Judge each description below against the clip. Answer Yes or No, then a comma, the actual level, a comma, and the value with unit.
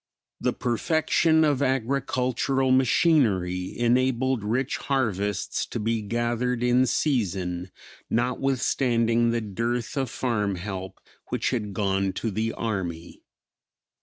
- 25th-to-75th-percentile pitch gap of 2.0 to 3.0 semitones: No, average, 4.1 semitones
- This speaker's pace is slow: Yes, slow, 105 wpm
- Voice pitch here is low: Yes, low, 120 Hz